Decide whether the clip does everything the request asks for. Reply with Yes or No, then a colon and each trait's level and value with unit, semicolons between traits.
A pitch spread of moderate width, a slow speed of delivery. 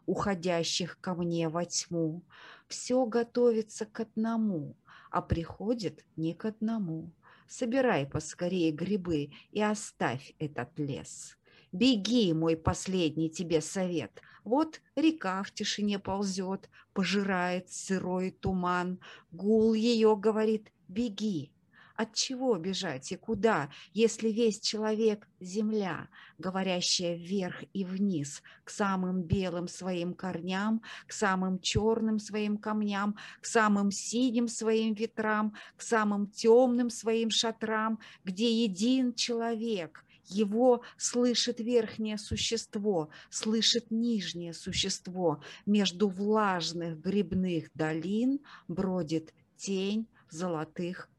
Yes: average, 4.1 semitones; slow, 105 wpm